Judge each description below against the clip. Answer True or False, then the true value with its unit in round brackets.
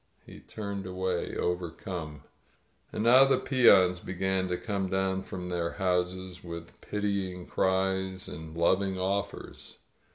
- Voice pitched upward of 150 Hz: False (95 Hz)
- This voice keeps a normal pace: False (125 wpm)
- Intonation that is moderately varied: False (1.3 semitones)